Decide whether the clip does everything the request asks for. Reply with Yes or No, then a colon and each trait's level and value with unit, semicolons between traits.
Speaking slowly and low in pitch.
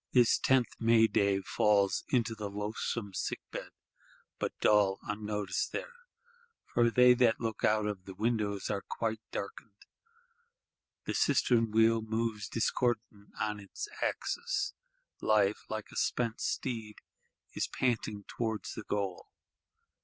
Yes: slow, 130 wpm; low, 110 Hz